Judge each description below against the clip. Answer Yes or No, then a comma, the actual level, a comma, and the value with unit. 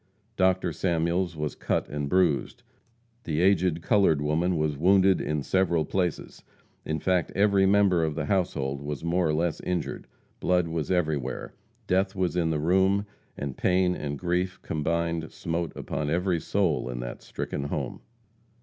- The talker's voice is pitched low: Yes, very low, 85 Hz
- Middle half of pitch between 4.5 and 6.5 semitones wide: No, average, 3.2 semitones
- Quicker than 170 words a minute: No, average, 155 wpm